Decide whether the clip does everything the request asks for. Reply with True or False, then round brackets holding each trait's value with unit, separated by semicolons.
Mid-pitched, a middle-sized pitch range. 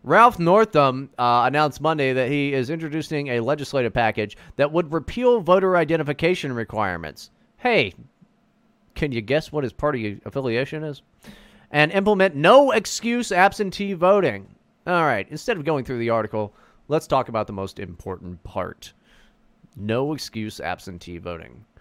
False (145 Hz; 8.2 semitones)